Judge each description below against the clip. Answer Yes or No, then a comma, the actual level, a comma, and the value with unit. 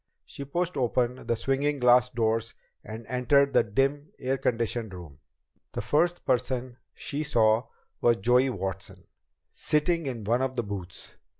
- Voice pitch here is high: No, low, 125 Hz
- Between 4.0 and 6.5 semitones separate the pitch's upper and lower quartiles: No, average, 3.5 semitones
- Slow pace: No, average, 145 wpm